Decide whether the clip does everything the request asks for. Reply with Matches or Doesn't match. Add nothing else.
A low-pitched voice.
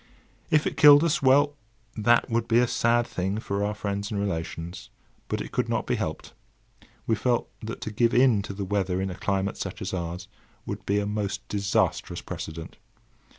Matches